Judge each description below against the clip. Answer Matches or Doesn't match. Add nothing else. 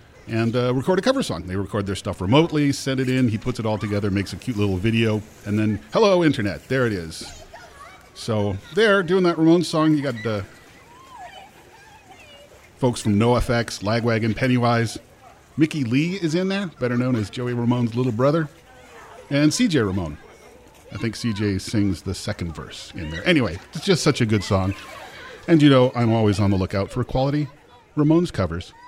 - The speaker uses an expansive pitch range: Matches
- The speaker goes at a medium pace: Matches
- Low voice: Matches